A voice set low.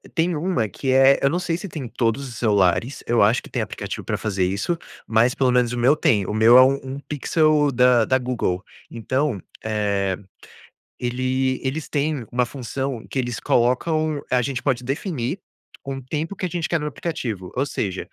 Yes: low, 130 Hz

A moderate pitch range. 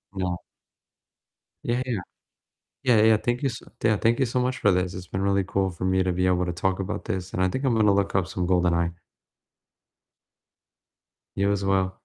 Yes: average, 3.0 semitones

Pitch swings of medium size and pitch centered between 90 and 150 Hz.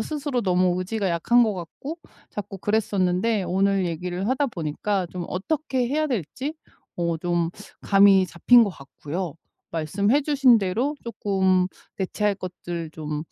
No: average, 4.9 semitones; high, 195 Hz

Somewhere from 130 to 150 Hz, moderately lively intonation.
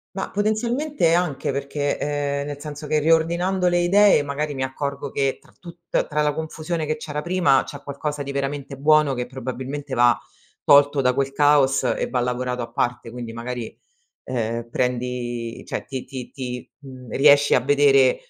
Yes: medium, 140 Hz; average, 3.1 semitones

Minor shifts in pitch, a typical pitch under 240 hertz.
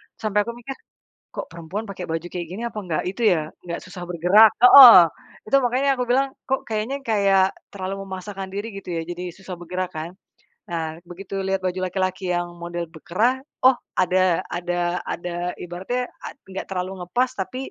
No: average, 3.6 semitones; medium, 185 Hz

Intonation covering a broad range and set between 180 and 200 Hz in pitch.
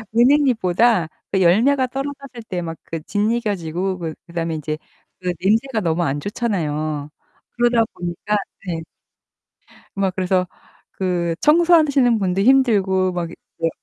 Yes: wide, 5.7 semitones; high, 190 Hz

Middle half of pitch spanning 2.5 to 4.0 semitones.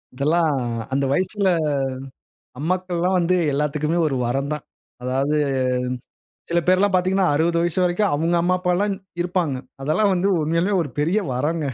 Yes: average, 3.6 semitones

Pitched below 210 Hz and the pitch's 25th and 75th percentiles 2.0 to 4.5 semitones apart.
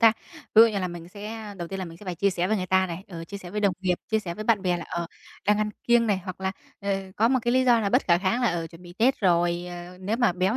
Yes: high, 190 Hz; average, 3.7 semitones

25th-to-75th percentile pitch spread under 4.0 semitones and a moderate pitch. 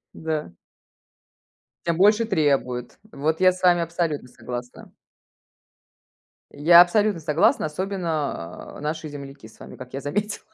No: average, 4.4 semitones; medium, 155 Hz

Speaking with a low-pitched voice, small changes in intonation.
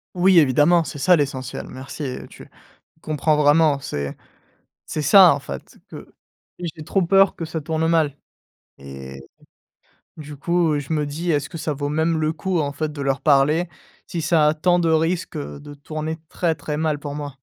No: medium, 155 Hz; narrow, 2.3 semitones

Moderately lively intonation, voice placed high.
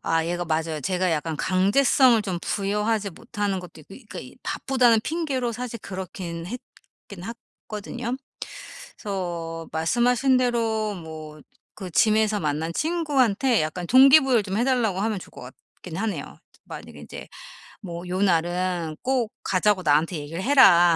No: wide, 5.8 semitones; high, 195 Hz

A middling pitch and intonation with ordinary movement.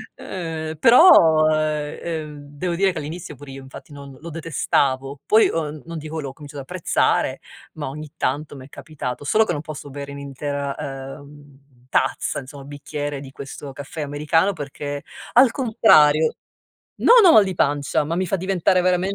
Yes: medium, 150 Hz; average, 3.0 semitones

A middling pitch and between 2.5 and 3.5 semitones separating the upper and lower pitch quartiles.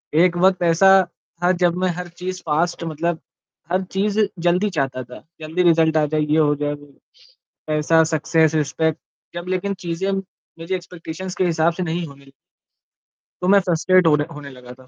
Yes: medium, 165 Hz; average, 2.8 semitones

